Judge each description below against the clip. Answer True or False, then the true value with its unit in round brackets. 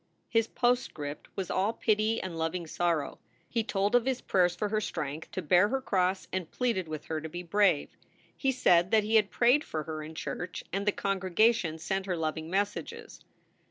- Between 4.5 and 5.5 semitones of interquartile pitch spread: True (4.8 semitones)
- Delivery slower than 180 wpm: False (195 wpm)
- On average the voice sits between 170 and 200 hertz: True (190 Hz)